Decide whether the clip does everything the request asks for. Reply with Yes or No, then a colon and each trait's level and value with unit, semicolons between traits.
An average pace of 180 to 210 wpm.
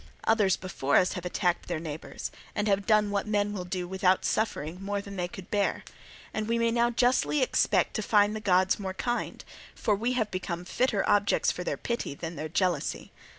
Yes: average, 200 wpm